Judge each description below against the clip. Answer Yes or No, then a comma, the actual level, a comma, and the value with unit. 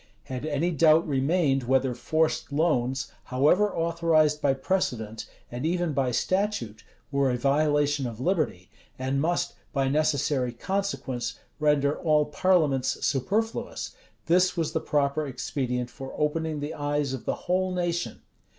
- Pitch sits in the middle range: Yes, medium, 145 Hz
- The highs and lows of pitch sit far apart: No, average, 4.0 semitones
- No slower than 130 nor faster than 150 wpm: Yes, average, 140 wpm